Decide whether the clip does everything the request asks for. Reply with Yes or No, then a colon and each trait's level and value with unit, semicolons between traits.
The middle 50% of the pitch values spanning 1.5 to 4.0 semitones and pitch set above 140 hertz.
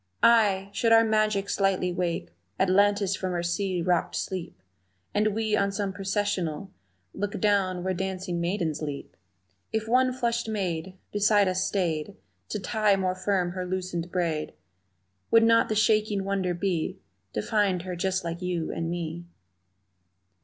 Yes: average, 2.8 semitones; high, 190 Hz